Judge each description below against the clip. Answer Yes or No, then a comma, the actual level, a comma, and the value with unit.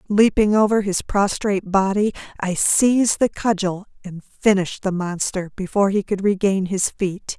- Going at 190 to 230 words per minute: No, average, 155 wpm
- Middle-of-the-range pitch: No, high, 195 Hz